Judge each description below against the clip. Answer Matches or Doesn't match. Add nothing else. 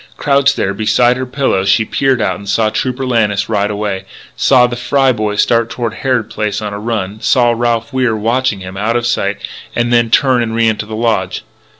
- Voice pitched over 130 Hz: Doesn't match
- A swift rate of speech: Matches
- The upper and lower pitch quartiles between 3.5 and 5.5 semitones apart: Doesn't match